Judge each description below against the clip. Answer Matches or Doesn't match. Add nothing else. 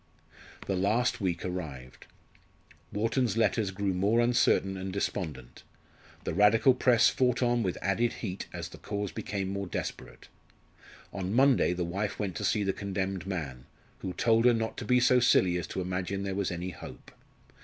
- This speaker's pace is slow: Doesn't match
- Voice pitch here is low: Matches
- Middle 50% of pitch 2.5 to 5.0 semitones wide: Matches